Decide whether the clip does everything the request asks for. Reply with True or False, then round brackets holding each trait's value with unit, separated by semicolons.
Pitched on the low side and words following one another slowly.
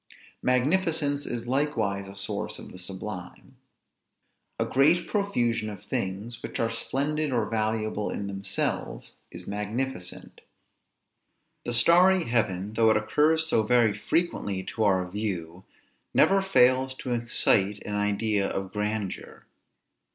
True (110 Hz; 125 wpm)